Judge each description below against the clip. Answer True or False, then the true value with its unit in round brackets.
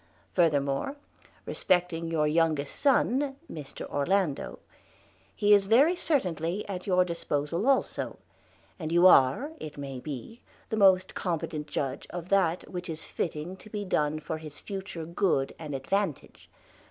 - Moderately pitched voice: True (170 Hz)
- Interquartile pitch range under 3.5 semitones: False (4.7 semitones)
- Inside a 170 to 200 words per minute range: False (140 wpm)